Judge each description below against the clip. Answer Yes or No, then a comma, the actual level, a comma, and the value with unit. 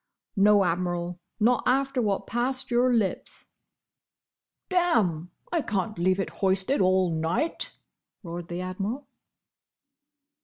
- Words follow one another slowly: Yes, slow, 110 wpm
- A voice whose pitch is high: Yes, high, 195 Hz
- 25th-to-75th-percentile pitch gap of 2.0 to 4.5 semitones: No, wide, 5.6 semitones